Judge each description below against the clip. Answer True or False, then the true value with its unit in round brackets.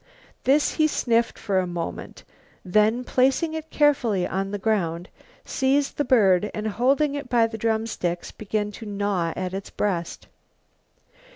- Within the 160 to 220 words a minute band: False (150 wpm)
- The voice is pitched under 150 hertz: False (215 Hz)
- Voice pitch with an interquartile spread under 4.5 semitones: False (5.2 semitones)